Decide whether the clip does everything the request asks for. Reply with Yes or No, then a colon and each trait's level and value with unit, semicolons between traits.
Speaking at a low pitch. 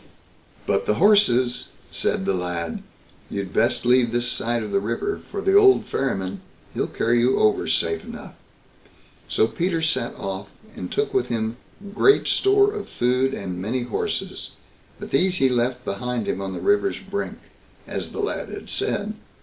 Yes: low, 125 Hz